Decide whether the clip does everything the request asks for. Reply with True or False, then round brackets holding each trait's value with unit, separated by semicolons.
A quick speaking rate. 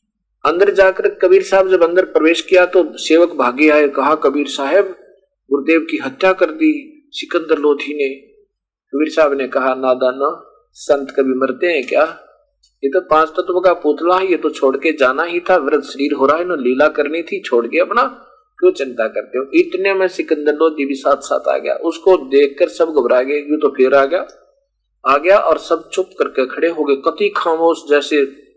True (205 wpm)